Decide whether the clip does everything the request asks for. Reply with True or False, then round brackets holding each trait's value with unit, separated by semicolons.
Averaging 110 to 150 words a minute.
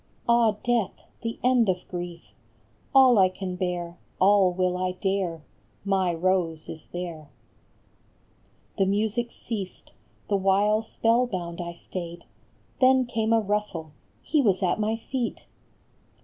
True (135 wpm)